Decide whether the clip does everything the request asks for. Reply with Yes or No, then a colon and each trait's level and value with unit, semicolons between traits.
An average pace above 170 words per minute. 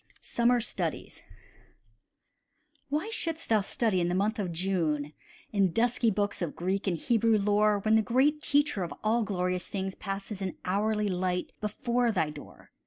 No: average, 160 wpm